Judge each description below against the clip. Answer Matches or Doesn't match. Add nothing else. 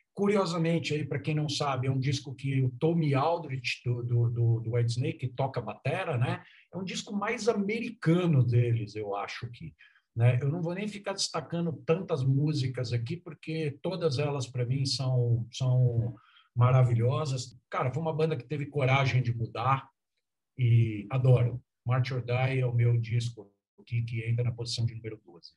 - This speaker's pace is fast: Doesn't match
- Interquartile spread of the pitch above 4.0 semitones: Matches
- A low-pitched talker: Matches